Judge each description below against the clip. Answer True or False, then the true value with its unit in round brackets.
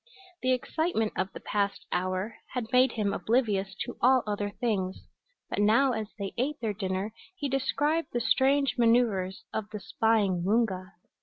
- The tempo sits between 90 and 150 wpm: False (160 wpm)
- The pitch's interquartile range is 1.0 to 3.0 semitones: False (4.2 semitones)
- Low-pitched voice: False (220 Hz)